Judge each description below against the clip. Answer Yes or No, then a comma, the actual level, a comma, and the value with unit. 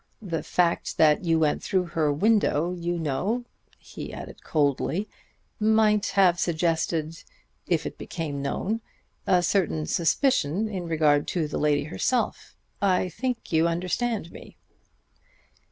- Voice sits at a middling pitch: Yes, medium, 170 Hz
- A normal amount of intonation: Yes, average, 4.2 semitones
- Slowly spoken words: Yes, slow, 130 wpm